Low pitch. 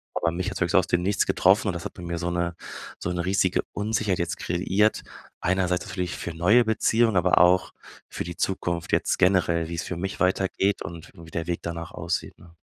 Yes: very low, 90 Hz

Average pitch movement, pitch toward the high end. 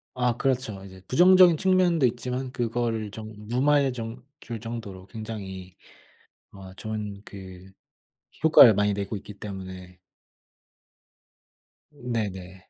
No: average, 4.5 semitones; low, 110 Hz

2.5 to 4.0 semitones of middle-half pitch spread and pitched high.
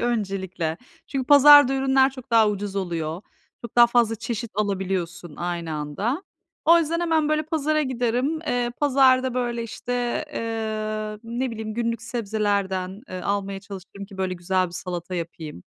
No: average, 5.1 semitones; high, 220 Hz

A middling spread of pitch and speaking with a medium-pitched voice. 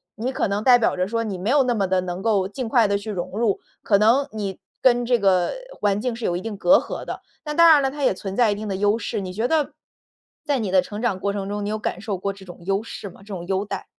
No: average, 3.7 semitones; high, 205 Hz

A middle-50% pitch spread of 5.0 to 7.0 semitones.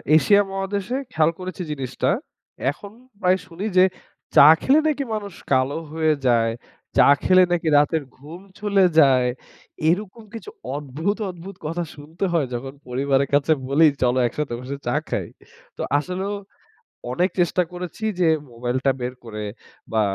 Yes: wide, 5.6 semitones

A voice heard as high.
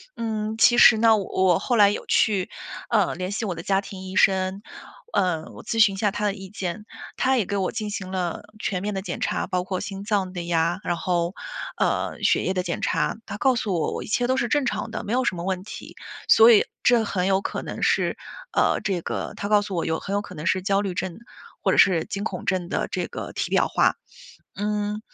Yes: high, 195 Hz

